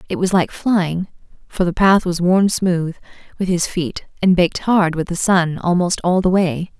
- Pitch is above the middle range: No, medium, 180 Hz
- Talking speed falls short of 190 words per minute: No, fast, 205 wpm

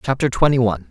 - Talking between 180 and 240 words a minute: Yes, average, 200 wpm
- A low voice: Yes, low, 115 Hz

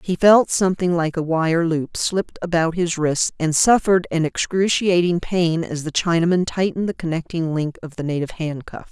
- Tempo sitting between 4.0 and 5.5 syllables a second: Yes, 5.2 syllables/s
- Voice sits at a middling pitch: Yes, medium, 170 Hz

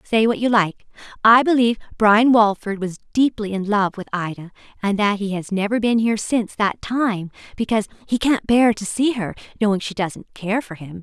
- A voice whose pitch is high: Yes, high, 210 Hz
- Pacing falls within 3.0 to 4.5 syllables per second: No, 5.4 syllables/s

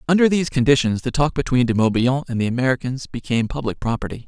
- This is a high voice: No, low, 130 Hz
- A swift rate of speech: No, average, 195 wpm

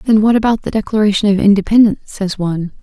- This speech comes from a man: No, female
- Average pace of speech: Yes, average, 190 wpm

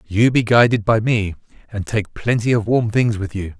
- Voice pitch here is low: Yes, low, 110 Hz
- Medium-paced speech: No, fast, 215 wpm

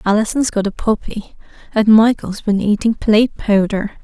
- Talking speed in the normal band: Yes, average, 150 wpm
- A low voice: No, high, 215 Hz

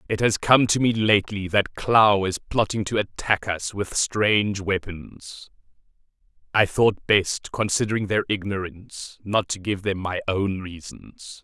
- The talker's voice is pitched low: Yes, low, 100 Hz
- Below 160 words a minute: Yes, average, 150 wpm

